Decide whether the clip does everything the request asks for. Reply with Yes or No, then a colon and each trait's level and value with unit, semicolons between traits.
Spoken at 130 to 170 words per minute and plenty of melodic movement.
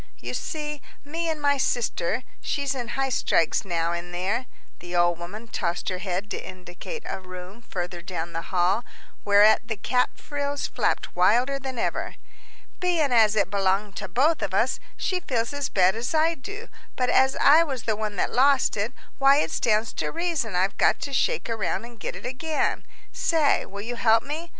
No: average, 190 wpm; wide, 6.9 semitones